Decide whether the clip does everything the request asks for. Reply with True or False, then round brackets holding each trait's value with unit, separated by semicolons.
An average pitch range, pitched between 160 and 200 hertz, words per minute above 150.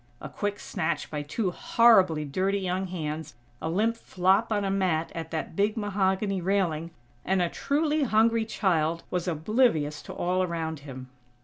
True (4.2 semitones; 185 Hz; 165 wpm)